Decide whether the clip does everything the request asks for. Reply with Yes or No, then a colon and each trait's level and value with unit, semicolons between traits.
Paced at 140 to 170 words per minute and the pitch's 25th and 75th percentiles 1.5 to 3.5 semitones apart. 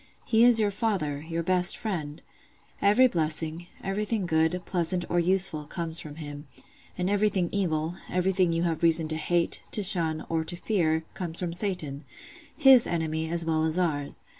Yes: average, 165 wpm; average, 3.2 semitones